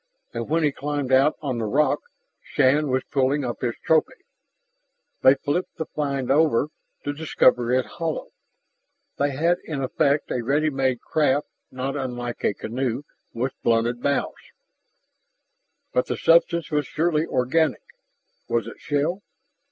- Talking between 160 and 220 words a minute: No, average, 145 wpm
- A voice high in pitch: No, medium, 140 Hz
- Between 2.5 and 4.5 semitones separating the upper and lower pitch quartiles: Yes, average, 3.1 semitones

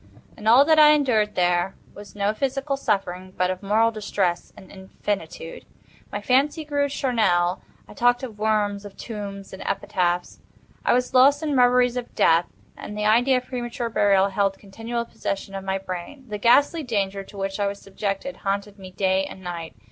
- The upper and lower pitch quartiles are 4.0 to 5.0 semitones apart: Yes, average, 4.3 semitones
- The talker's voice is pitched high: Yes, high, 205 Hz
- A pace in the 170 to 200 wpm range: Yes, average, 180 wpm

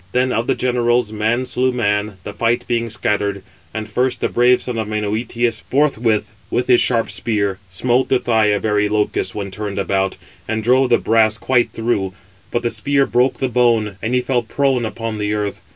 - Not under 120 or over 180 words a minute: No, average, 190 wpm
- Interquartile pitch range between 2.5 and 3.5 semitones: Yes, average, 2.8 semitones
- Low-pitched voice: Yes, low, 115 Hz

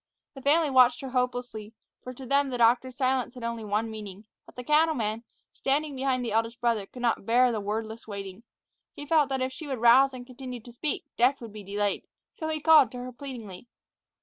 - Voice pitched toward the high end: Yes, high, 245 Hz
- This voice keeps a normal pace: No, fast, 210 wpm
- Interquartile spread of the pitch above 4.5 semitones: No, average, 3.1 semitones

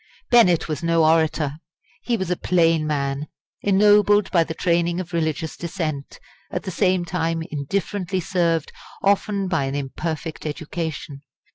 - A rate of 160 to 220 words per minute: No, average, 140 wpm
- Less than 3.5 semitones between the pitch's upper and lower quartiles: Yes, average, 3.0 semitones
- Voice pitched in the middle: Yes, medium, 165 Hz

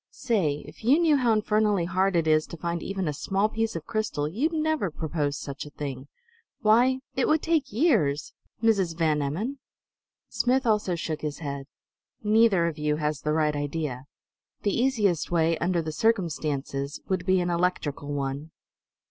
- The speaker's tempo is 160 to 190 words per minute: Yes, average, 170 wpm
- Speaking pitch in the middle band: Yes, medium, 175 Hz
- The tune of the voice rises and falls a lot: Yes, wide, 6.5 semitones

